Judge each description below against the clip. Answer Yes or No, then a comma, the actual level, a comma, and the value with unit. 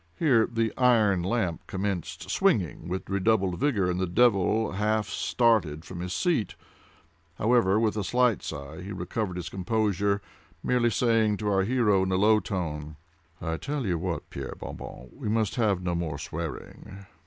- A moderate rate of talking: Yes, average, 165 wpm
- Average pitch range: Yes, average, 4.1 semitones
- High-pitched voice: No, low, 100 Hz